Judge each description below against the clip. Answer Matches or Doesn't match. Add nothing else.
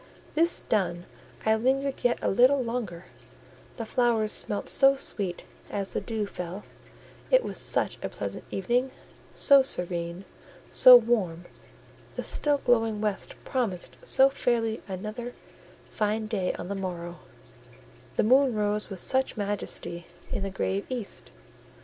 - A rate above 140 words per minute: Doesn't match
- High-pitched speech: Matches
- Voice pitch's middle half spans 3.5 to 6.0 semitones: Matches